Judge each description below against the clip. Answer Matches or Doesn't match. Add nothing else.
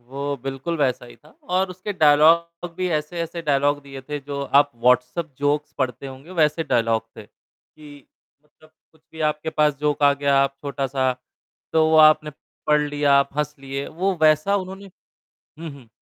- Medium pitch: Matches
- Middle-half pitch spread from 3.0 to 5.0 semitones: Doesn't match